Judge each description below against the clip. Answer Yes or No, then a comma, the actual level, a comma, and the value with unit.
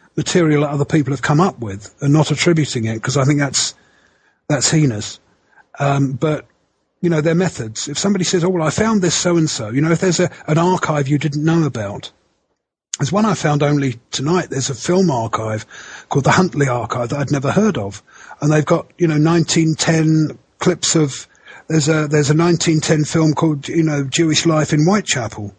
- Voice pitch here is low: No, medium, 155 Hz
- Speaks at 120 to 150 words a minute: No, average, 200 wpm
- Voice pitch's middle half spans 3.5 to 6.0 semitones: No, average, 3.1 semitones